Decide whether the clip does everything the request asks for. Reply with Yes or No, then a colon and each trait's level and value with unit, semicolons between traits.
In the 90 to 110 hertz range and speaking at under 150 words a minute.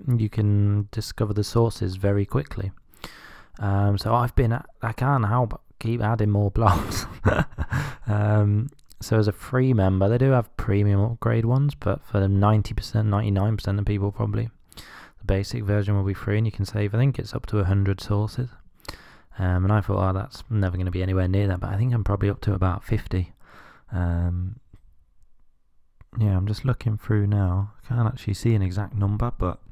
No: low, 105 Hz; average, 190 wpm